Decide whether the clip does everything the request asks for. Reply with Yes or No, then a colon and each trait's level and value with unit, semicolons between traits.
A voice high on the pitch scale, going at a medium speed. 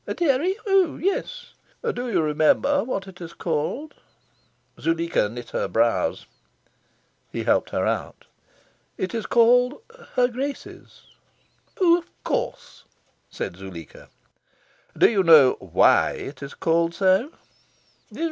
No: high, 200 Hz; slow, 120 wpm